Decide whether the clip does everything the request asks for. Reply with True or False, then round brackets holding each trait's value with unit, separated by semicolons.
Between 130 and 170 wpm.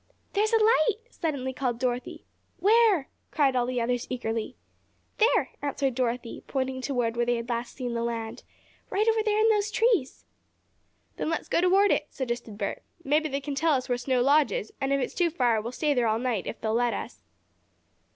False (195 wpm)